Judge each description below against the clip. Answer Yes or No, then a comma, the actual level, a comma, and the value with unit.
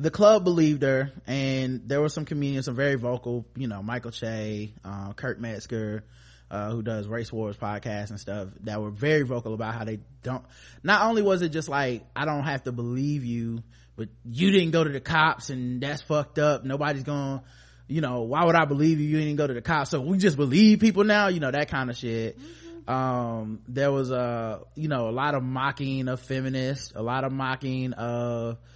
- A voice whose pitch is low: Yes, low, 130 Hz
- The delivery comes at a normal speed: No, fast, 215 wpm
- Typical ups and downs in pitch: Yes, average, 4.3 semitones